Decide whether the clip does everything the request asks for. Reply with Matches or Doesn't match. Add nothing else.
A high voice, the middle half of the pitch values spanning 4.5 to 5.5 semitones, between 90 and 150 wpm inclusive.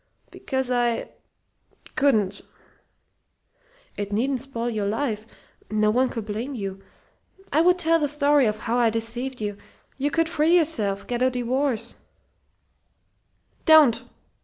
Matches